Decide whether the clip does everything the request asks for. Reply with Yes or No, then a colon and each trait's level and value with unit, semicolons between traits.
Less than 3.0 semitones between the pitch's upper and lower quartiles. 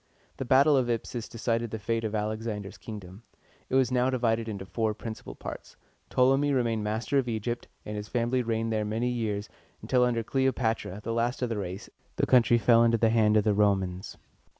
Yes: narrow, 2.5 semitones